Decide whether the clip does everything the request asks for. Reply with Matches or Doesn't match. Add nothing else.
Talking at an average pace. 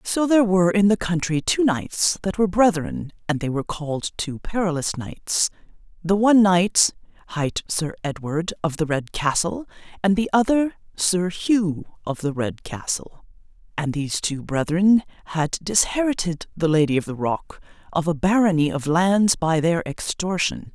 Matches